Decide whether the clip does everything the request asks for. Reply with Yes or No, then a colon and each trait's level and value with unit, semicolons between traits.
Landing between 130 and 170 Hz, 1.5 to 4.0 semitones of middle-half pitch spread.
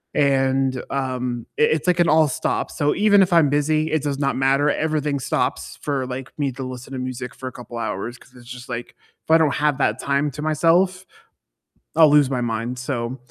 Yes: medium, 140 Hz; average, 3.1 semitones